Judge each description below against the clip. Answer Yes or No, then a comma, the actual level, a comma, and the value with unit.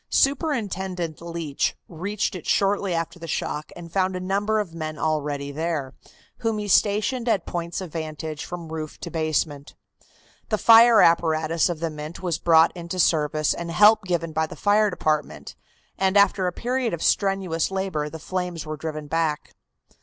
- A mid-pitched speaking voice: Yes, medium, 170 Hz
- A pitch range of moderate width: Yes, average, 3.8 semitones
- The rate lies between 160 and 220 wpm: Yes, average, 170 wpm